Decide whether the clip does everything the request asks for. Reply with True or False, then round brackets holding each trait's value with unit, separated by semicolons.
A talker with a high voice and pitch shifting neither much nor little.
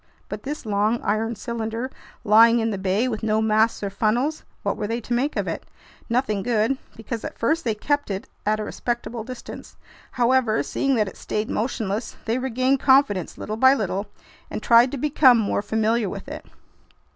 True (225 Hz; 3.1 semitones)